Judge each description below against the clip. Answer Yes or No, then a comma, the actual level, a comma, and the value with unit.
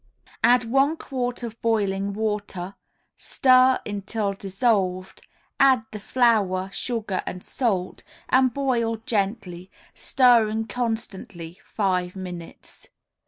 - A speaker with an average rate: No, slow, 100 wpm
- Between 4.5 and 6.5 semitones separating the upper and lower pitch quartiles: No, average, 4.1 semitones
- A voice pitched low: No, high, 215 Hz